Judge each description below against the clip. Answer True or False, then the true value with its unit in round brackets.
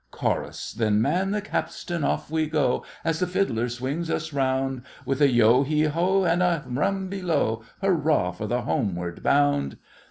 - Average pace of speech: True (160 wpm)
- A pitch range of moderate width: False (5.8 semitones)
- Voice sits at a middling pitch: True (145 Hz)